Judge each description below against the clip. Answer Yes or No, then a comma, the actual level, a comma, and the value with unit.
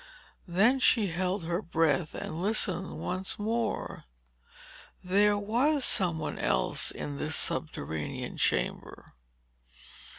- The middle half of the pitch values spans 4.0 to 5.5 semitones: Yes, average, 4.4 semitones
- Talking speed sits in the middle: No, slow, 105 wpm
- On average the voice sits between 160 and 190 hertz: Yes, medium, 185 Hz